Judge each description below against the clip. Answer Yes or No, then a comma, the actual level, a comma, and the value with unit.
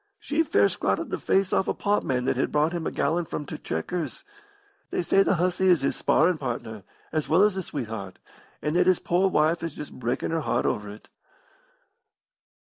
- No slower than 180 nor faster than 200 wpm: Yes, average, 195 wpm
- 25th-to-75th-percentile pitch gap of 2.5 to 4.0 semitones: No, wide, 5.5 semitones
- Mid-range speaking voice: Yes, medium, 160 Hz